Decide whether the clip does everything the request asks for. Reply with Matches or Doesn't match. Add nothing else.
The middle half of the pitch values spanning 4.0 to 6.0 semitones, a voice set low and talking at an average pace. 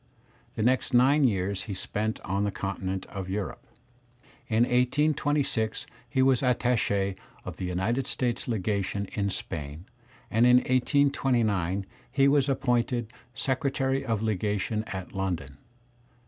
Doesn't match